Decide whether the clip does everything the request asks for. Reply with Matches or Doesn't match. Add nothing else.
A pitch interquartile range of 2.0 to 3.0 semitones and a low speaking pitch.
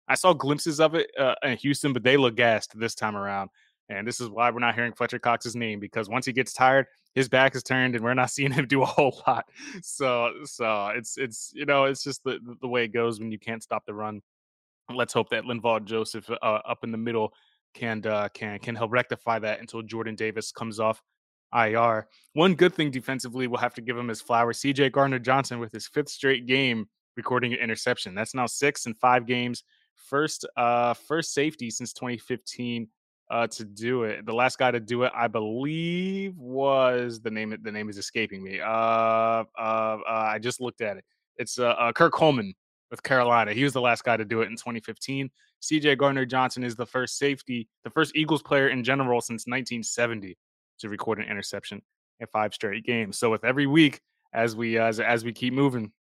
Matches